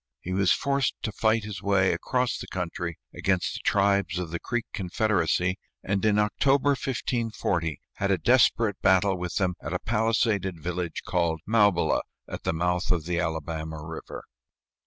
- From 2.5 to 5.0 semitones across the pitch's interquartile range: Yes, average, 3.9 semitones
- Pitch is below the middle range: Yes, very low, 95 Hz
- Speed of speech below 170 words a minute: Yes, average, 160 wpm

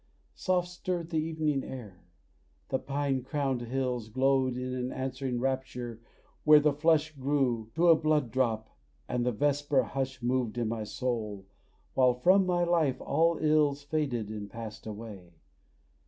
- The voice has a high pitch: No, low, 130 Hz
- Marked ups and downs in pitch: No, average, 3.9 semitones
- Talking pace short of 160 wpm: Yes, average, 150 wpm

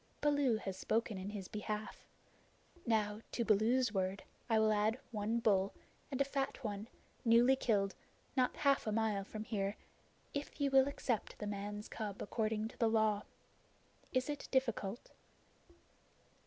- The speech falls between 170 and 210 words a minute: No, average, 150 wpm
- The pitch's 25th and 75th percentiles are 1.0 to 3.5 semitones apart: Yes, average, 3.2 semitones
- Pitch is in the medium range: No, high, 220 Hz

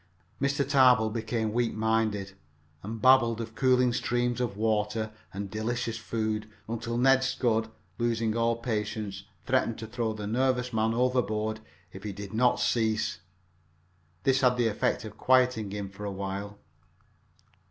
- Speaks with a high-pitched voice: No, low, 115 Hz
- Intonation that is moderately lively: No, narrow, 2.3 semitones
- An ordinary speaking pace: Yes, average, 145 wpm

